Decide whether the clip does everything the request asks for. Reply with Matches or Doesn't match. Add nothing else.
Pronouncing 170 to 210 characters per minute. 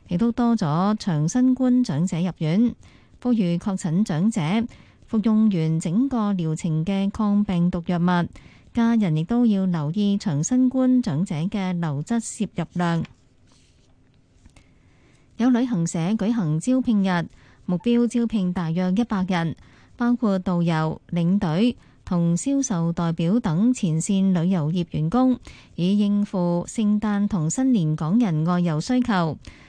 Matches